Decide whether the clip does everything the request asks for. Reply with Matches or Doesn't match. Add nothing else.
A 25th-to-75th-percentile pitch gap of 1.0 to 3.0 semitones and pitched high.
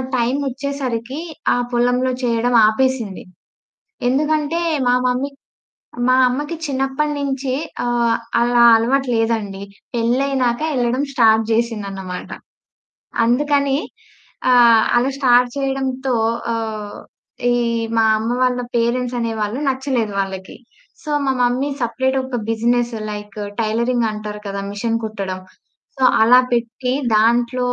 Matches